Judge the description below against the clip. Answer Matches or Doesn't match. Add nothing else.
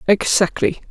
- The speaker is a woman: Matches